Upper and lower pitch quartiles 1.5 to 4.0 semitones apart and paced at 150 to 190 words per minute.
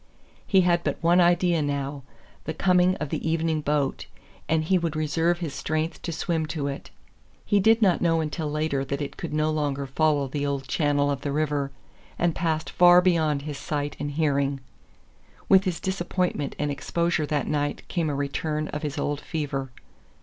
Yes: average, 2.9 semitones; average, 185 wpm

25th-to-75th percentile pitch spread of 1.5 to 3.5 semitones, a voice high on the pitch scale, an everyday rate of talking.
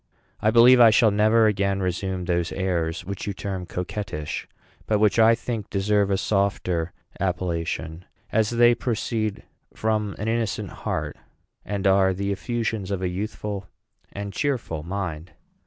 No: average, 3.0 semitones; low, 100 Hz; average, 145 wpm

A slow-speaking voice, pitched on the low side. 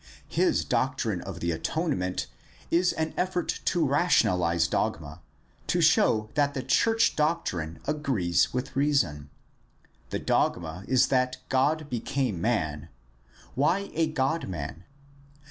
Yes: slow, 120 wpm; low, 130 Hz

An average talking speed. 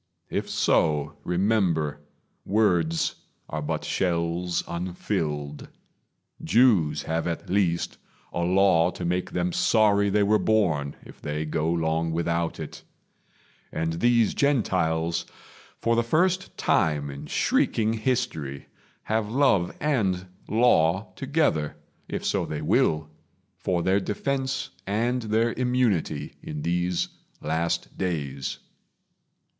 No: slow, 115 wpm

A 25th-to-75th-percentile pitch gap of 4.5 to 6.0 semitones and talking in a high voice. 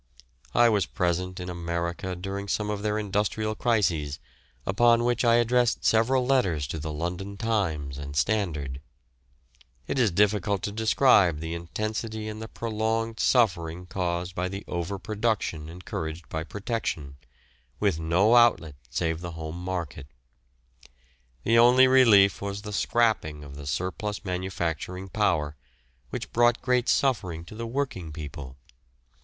No: average, 5.1 semitones; very low, 95 Hz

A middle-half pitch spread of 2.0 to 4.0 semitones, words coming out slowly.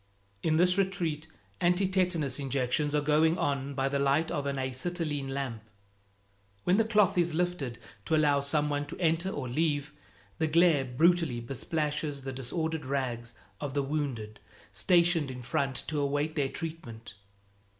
No: average, 3.4 semitones; average, 155 wpm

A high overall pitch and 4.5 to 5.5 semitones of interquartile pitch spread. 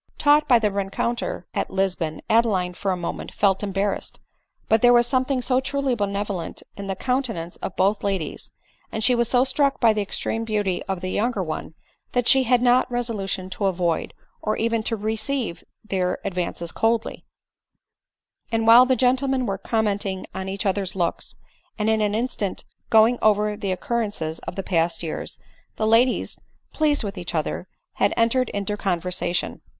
No: high, 210 Hz; average, 4.1 semitones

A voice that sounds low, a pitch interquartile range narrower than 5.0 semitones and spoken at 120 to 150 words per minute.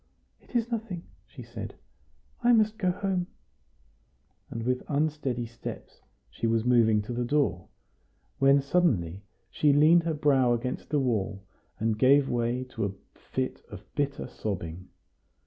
No: low, 130 Hz; wide, 5.4 semitones; average, 145 wpm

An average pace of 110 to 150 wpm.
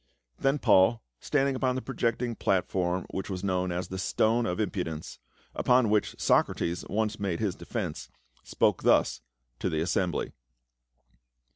Yes: average, 140 wpm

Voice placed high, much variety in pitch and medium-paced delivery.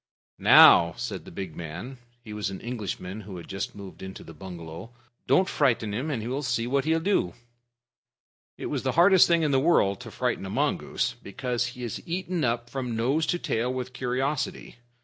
No: low, 120 Hz; wide, 6.0 semitones; average, 190 wpm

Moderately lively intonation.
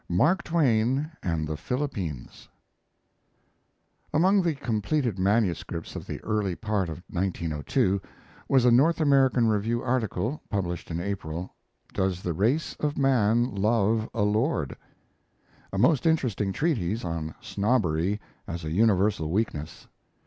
No: wide, 6.3 semitones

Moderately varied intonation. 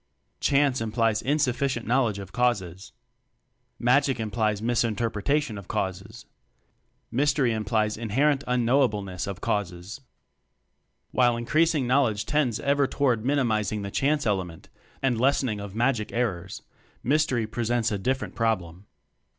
Yes: average, 4.3 semitones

